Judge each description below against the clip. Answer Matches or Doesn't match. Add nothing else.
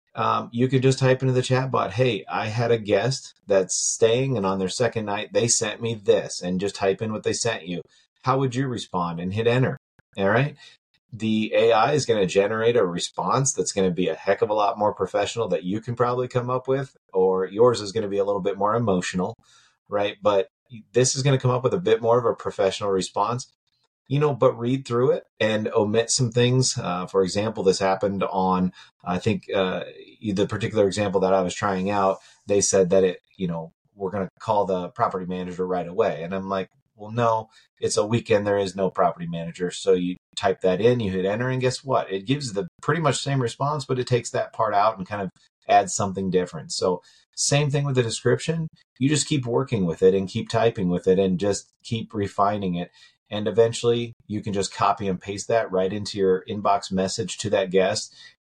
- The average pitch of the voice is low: Matches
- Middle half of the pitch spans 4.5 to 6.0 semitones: Matches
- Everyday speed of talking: Doesn't match